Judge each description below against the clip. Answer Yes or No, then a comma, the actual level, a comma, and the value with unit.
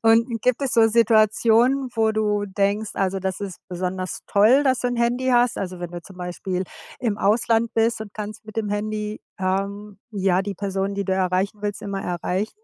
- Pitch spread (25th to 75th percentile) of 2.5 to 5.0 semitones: Yes, average, 2.8 semitones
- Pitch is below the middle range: No, high, 205 Hz